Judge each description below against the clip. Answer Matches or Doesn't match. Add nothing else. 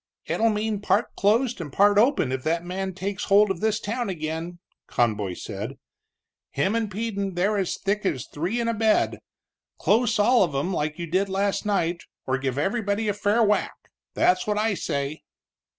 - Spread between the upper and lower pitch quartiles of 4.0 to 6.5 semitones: Matches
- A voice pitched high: Matches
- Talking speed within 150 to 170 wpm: Doesn't match